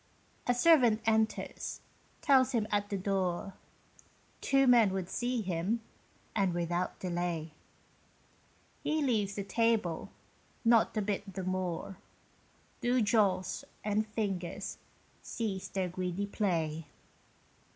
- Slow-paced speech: Yes, slow, 110 wpm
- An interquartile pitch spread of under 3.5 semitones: No, average, 3.8 semitones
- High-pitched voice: Yes, high, 200 Hz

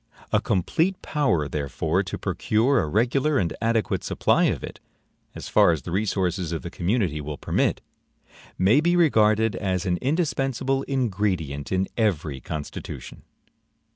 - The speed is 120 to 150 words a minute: Yes, average, 140 wpm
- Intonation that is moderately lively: No, wide, 7.3 semitones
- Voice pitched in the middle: No, low, 100 Hz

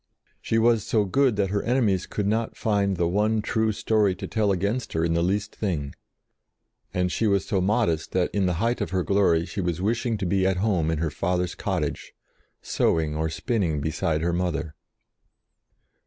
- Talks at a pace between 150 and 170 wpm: No, average, 185 wpm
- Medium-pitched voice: No, very low, 95 Hz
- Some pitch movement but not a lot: Yes, average, 4.0 semitones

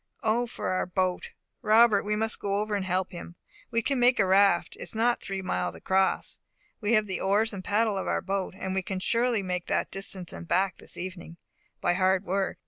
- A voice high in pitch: Yes, high, 195 Hz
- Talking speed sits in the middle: No, fast, 220 wpm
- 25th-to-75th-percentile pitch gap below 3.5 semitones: Yes, narrow, 2.6 semitones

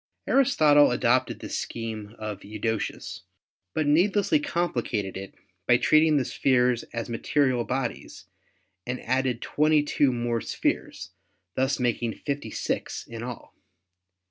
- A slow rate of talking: Yes, slow, 115 wpm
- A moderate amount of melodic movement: Yes, average, 4.1 semitones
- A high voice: No, low, 125 Hz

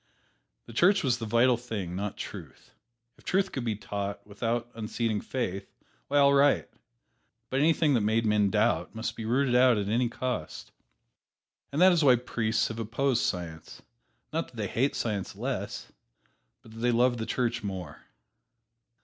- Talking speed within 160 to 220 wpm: Yes, average, 165 wpm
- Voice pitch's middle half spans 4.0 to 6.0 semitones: No, average, 3.3 semitones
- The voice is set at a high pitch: No, low, 115 Hz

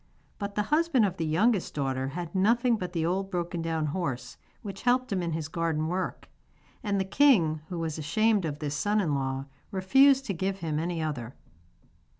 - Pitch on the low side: No, medium, 175 Hz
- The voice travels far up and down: No, average, 4.8 semitones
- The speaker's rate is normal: Yes, average, 190 wpm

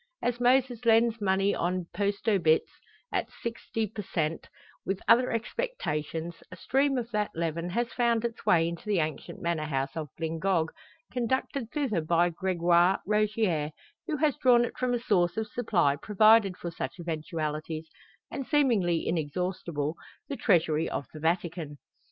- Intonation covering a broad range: Yes, wide, 6.0 semitones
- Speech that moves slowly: No, average, 150 wpm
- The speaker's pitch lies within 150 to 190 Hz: Yes, medium, 185 Hz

